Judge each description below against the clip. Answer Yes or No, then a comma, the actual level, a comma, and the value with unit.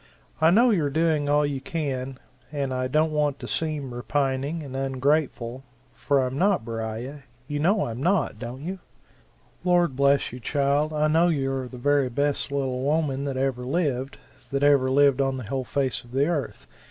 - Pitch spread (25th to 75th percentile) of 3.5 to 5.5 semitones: No, narrow, 2.6 semitones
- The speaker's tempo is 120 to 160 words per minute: No, average, 185 wpm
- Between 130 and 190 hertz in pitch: Yes, medium, 140 Hz